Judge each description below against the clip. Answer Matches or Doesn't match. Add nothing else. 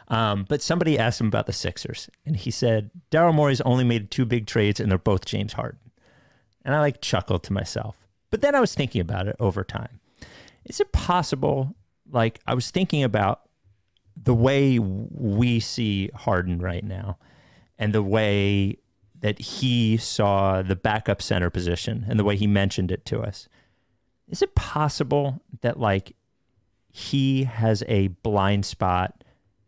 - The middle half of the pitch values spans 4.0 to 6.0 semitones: Matches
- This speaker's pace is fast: Doesn't match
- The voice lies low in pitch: Matches